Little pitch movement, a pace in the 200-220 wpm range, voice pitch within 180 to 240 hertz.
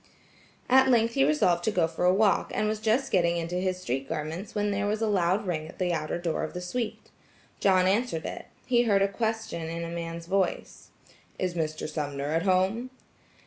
No: average, 4.1 semitones; fast, 205 wpm; medium, 185 Hz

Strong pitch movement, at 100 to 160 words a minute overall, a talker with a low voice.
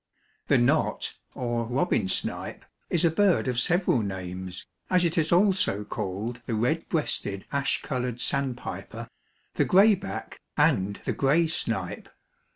Yes: wide, 8.3 semitones; average, 145 wpm; low, 125 Hz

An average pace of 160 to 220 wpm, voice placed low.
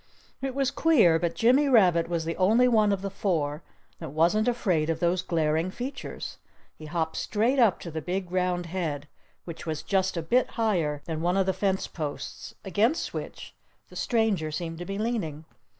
No: average, 180 wpm; medium, 180 Hz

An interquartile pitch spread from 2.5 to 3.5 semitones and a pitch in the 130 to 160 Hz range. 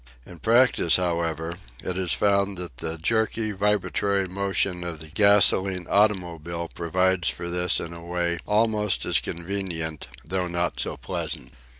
No: average, 2.8 semitones; very low, 90 Hz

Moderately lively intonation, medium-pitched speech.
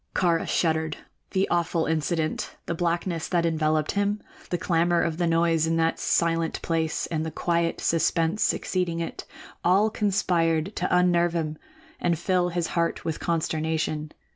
No: narrow, 1.5 semitones; medium, 170 Hz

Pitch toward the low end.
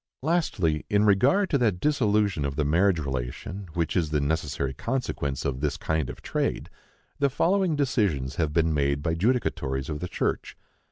Yes: very low, 85 Hz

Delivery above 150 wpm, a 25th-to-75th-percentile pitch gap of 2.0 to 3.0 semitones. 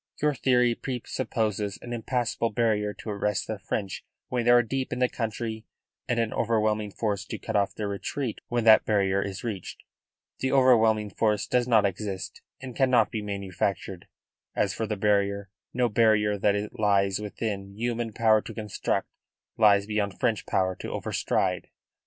Yes: average, 170 wpm; average, 2.7 semitones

